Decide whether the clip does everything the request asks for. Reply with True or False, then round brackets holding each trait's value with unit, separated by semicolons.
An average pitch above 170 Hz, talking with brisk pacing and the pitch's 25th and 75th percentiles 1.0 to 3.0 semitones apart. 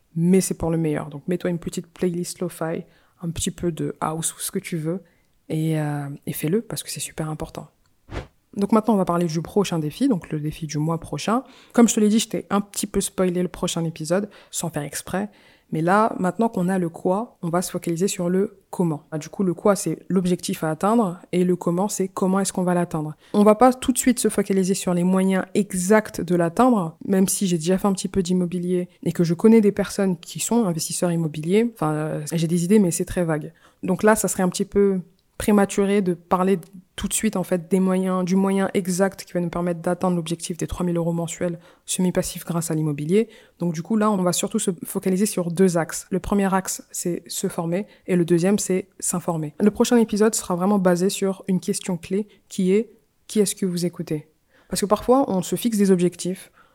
True (185 Hz; 230 wpm; 2.6 semitones)